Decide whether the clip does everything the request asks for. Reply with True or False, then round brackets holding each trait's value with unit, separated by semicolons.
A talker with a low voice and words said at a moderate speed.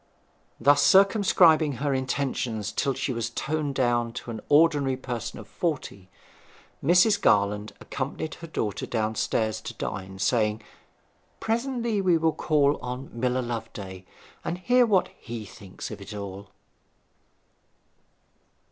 False (130 Hz; 125 wpm)